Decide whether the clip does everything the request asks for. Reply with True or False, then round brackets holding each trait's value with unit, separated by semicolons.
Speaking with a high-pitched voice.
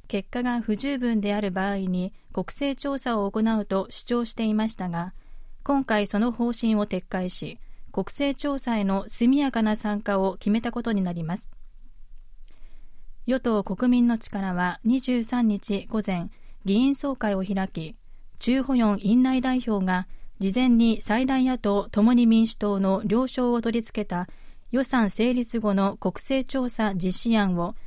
True (220 Hz)